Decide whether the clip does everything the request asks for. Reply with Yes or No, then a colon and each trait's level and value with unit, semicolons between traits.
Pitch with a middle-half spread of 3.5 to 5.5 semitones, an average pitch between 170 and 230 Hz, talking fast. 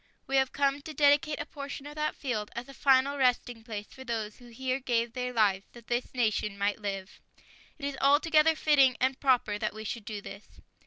No: average, 4.1 semitones; very high, 255 Hz; fast, 210 wpm